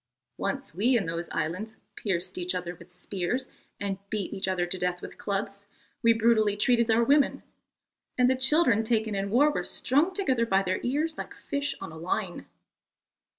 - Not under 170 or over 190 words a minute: Yes, average, 180 wpm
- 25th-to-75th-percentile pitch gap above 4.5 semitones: Yes, average, 5.2 semitones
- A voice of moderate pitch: No, high, 215 Hz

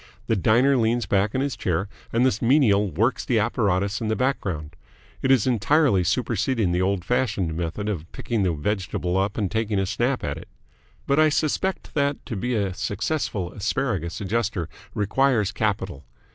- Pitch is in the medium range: No, low, 105 Hz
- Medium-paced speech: Yes, average, 175 wpm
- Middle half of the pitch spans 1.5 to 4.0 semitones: No, average, 4.7 semitones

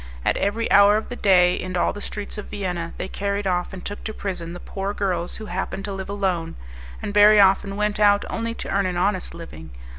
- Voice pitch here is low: No, high, 195 Hz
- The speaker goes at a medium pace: No, fast, 230 wpm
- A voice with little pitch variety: Yes, narrow, 2.3 semitones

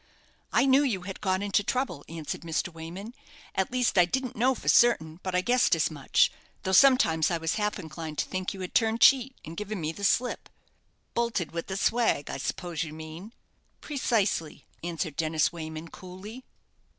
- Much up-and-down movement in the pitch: Yes, wide, 6.1 semitones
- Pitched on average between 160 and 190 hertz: Yes, medium, 185 Hz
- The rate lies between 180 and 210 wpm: Yes, average, 185 wpm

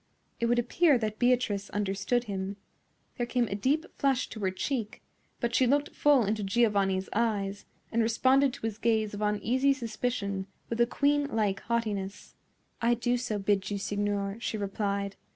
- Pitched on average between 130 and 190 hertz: No, high, 220 Hz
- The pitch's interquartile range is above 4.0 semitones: No, average, 3.4 semitones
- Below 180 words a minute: Yes, average, 165 wpm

